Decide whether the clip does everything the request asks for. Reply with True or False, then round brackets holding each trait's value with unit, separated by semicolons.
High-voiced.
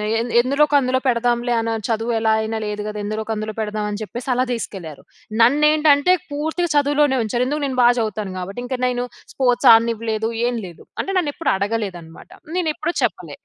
True (235 Hz)